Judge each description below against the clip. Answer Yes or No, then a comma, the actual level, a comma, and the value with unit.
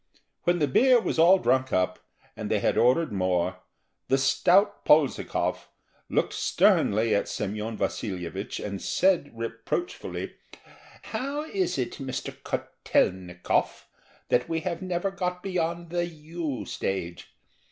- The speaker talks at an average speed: No, slow, 125 wpm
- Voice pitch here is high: No, medium, 145 Hz